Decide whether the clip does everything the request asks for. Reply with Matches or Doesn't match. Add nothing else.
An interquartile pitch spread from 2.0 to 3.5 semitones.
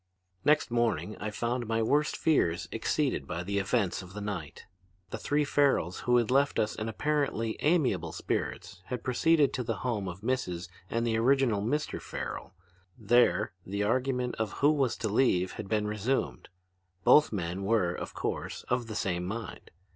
Doesn't match